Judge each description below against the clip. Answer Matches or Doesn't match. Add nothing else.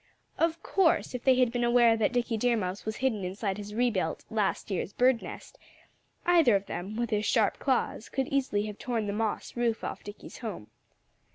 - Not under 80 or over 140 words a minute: Doesn't match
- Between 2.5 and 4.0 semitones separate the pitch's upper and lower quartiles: Matches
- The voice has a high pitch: Matches